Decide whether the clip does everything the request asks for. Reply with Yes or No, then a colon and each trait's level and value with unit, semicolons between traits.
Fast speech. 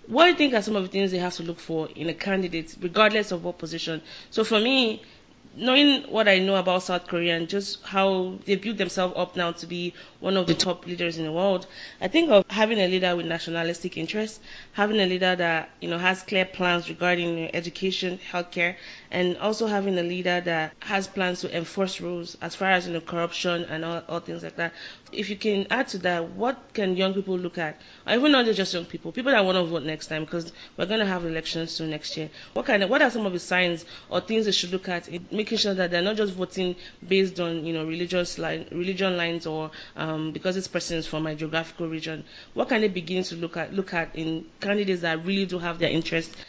Yes: fast, 235 wpm